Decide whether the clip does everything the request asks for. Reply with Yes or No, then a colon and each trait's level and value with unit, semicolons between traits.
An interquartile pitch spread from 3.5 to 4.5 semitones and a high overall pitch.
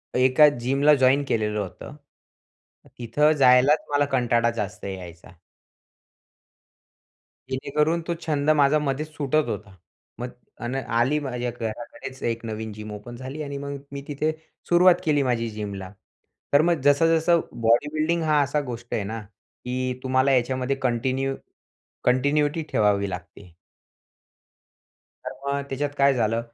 No: average, 3.9 semitones; low, 130 Hz